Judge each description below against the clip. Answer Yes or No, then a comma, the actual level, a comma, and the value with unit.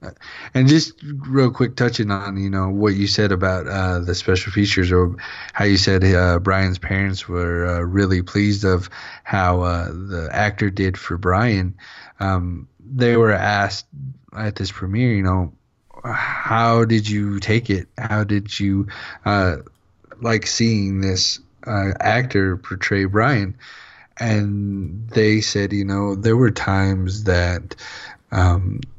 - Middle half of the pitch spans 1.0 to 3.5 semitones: Yes, narrow, 2.6 semitones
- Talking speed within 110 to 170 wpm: Yes, average, 145 wpm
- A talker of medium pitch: No, low, 100 Hz